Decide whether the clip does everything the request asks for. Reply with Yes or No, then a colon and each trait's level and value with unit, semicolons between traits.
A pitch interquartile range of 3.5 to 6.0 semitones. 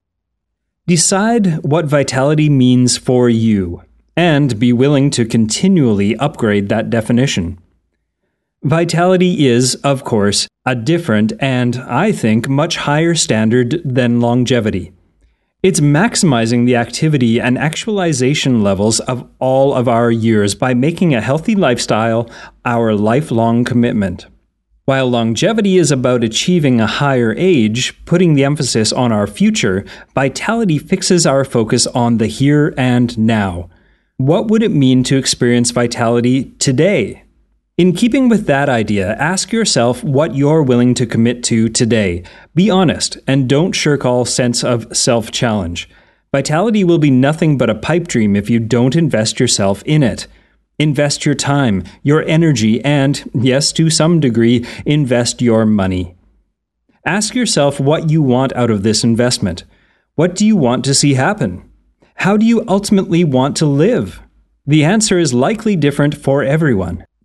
Yes: average, 5.1 semitones